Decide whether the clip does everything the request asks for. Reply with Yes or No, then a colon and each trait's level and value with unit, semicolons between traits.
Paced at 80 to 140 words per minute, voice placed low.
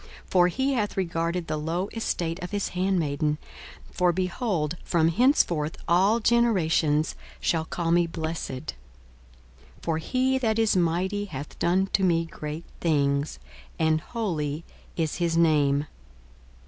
No: slow, 135 wpm; medium, 170 Hz